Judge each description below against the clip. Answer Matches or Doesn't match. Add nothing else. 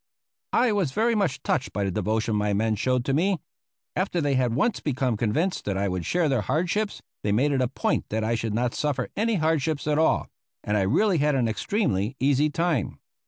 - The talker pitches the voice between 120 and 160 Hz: Matches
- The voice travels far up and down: Matches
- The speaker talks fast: Matches